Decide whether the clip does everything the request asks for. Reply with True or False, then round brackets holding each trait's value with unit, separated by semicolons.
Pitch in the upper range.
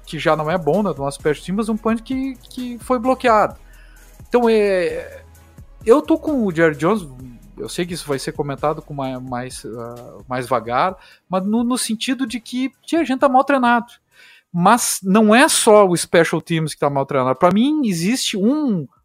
True (205 Hz)